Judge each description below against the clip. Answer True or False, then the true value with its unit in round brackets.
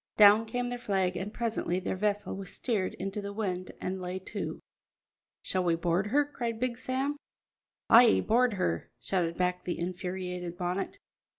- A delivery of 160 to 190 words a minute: True (165 wpm)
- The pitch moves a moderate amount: True (4.0 semitones)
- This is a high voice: True (195 Hz)